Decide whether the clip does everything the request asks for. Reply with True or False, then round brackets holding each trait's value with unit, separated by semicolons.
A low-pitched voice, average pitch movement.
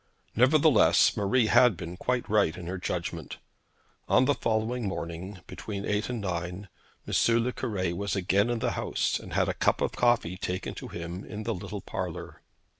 True (100 Hz; 4.7 semitones)